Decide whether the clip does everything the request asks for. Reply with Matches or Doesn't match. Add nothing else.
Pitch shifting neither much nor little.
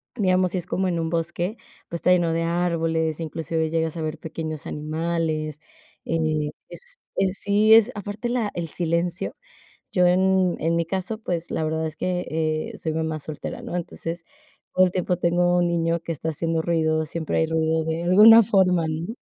Doesn't match